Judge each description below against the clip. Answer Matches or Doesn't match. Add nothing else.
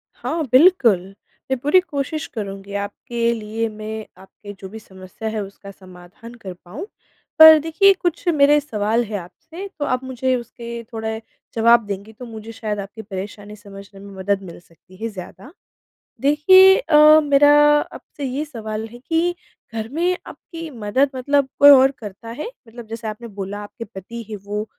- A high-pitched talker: Matches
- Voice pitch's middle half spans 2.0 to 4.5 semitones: Doesn't match